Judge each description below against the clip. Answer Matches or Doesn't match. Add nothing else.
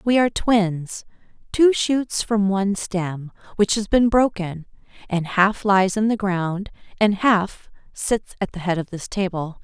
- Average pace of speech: Matches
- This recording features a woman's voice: Matches